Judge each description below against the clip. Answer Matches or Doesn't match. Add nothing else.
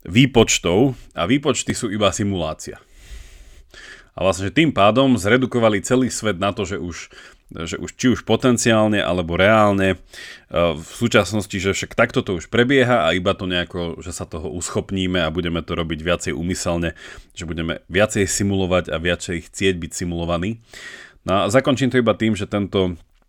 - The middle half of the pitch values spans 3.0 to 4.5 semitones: Matches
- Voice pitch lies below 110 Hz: Matches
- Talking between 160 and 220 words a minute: Matches